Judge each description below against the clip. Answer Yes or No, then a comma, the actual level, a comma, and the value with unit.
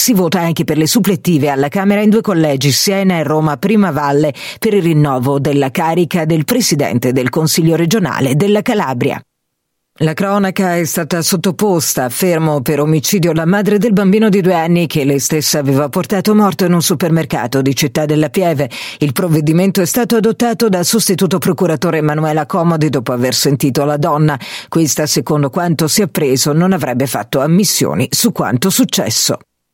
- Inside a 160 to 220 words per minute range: Yes, fast, 170 wpm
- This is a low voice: No, medium, 165 Hz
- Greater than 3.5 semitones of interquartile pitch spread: Yes, average, 4.6 semitones